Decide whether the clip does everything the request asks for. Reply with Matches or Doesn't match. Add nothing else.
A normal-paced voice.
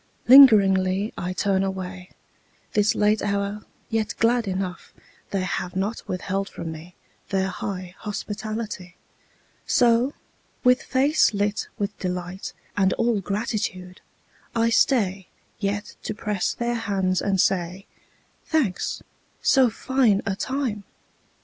Doesn't match